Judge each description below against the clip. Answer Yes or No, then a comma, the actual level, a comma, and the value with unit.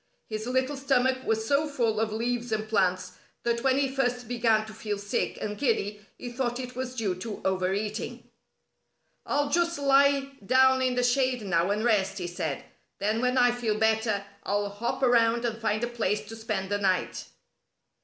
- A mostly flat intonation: No, average, 3.4 semitones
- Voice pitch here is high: Yes, high, 230 Hz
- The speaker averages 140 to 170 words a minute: No, average, 185 wpm